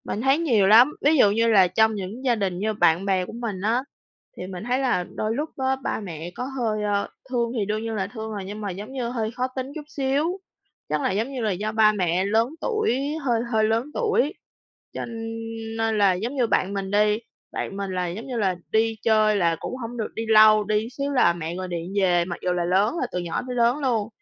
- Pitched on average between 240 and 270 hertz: No, high, 215 Hz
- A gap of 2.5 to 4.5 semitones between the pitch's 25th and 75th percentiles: Yes, average, 4.0 semitones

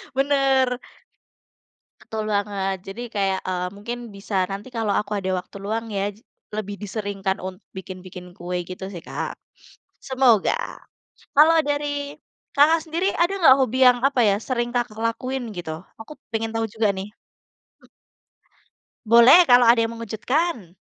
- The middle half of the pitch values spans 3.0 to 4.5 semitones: No, average, 4.9 semitones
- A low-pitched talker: No, high, 225 Hz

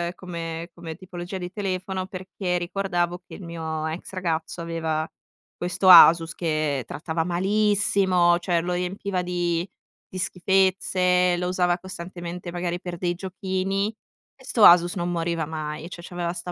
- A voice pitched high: No, medium, 175 Hz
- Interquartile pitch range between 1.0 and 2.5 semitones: Yes, narrow, 1.6 semitones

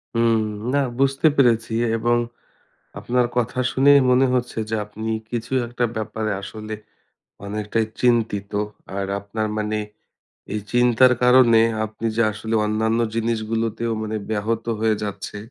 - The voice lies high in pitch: No, low, 115 Hz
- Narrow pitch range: Yes, narrow, 1.9 semitones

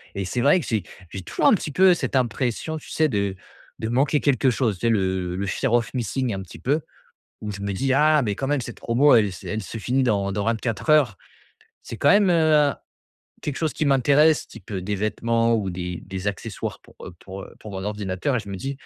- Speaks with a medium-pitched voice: No, low, 115 Hz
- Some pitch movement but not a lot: No, wide, 5.8 semitones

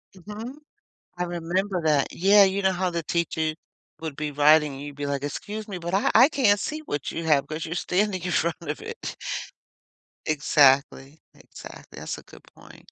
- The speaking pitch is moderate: Yes, medium, 170 Hz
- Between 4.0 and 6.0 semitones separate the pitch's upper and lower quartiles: Yes, average, 4.8 semitones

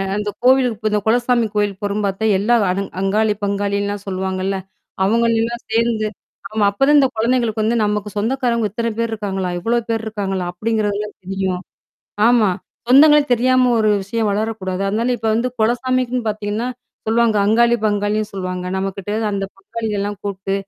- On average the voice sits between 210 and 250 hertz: Yes, high, 215 Hz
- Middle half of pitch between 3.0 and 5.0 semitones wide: No, narrow, 2.6 semitones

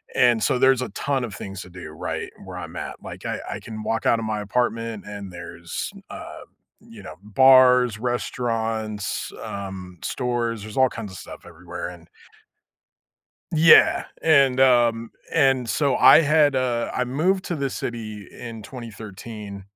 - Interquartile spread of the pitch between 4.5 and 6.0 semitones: No, average, 3.8 semitones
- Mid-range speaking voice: No, low, 115 Hz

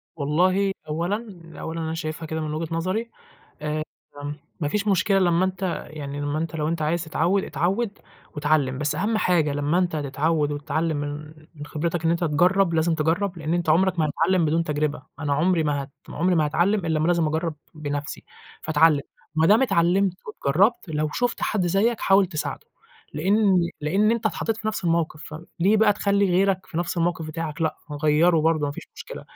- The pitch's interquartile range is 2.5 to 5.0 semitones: Yes, average, 3.5 semitones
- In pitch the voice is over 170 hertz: No, medium, 165 Hz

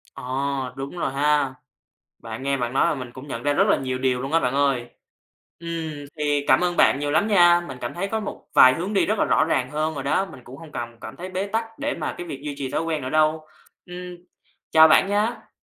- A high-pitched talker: No, medium, 150 Hz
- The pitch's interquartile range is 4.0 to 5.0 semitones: Yes, average, 4.7 semitones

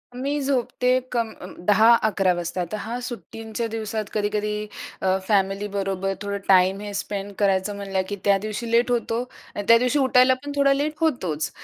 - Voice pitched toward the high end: Yes, high, 210 Hz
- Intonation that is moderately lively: Yes, average, 3.5 semitones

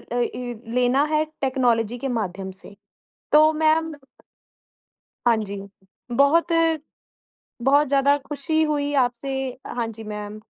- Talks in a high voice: Yes, very high, 265 Hz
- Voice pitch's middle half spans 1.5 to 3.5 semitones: No, average, 4.2 semitones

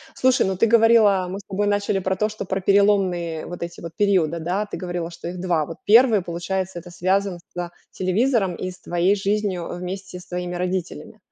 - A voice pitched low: No, medium, 185 Hz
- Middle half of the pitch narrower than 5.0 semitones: Yes, narrow, 2.4 semitones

